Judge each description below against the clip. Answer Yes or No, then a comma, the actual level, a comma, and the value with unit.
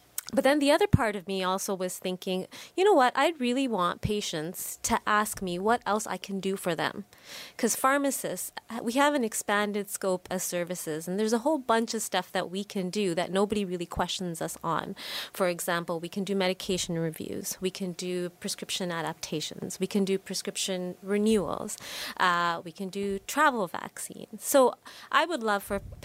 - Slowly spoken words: No, average, 185 wpm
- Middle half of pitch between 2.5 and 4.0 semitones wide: Yes, average, 3.2 semitones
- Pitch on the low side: No, high, 195 Hz